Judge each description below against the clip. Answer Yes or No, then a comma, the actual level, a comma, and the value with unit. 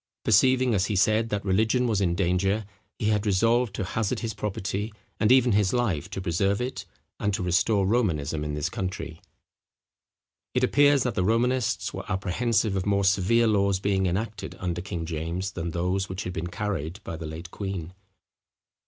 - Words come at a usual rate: Yes, average, 180 wpm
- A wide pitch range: No, average, 3.4 semitones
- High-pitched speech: No, low, 100 Hz